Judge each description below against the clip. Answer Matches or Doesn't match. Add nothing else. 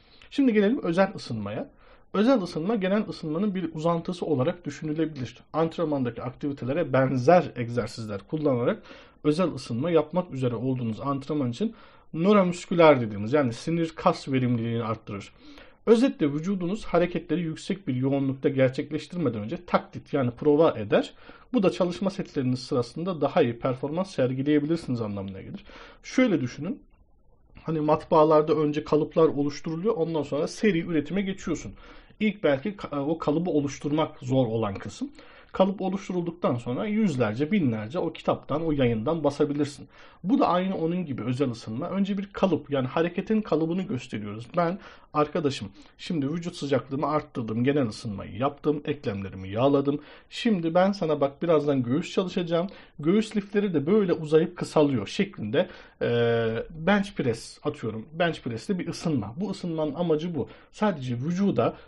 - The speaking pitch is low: Doesn't match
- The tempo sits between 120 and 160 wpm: Matches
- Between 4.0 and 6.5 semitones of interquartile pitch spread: Matches